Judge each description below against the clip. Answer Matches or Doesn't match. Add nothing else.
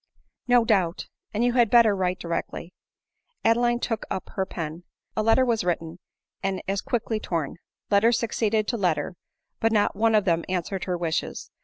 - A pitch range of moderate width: Matches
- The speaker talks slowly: Doesn't match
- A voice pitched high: Matches